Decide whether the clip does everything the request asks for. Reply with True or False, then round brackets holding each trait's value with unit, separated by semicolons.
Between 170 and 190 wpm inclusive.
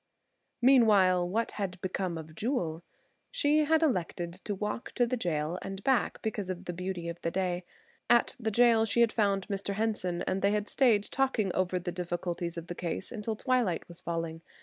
True (185 wpm)